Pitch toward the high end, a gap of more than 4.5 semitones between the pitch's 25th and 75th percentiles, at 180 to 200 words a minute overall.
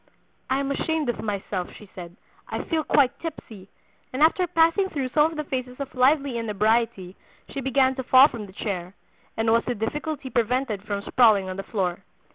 Yes: very high, 250 Hz; average, 5.3 semitones; average, 190 wpm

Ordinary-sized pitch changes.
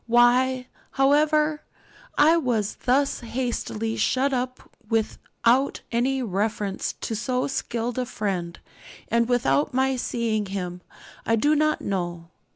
Yes: average, 3.7 semitones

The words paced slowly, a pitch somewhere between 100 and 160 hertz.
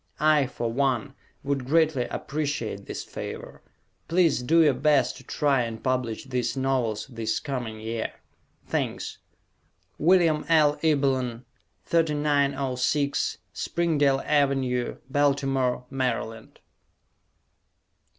Yes: slow, 100 wpm; low, 135 Hz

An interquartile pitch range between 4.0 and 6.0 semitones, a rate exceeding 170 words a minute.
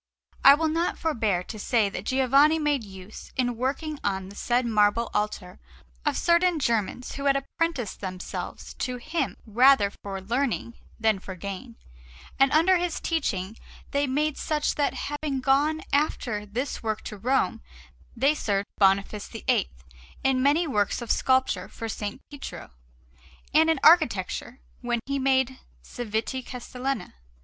No: average, 5.2 semitones; average, 145 wpm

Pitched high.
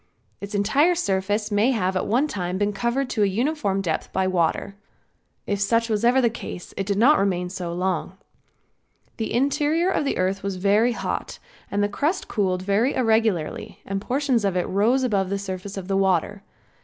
Yes: high, 205 Hz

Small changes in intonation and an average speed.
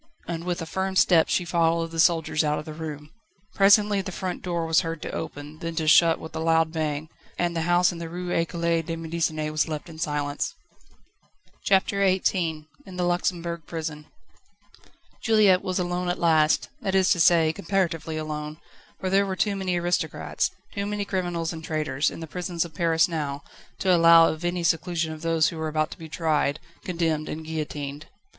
Yes: narrow, 2.1 semitones; average, 190 wpm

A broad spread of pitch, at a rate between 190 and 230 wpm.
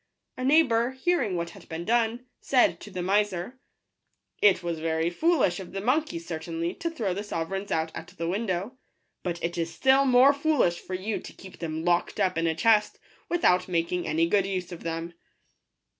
Yes: wide, 6.1 semitones; average, 195 wpm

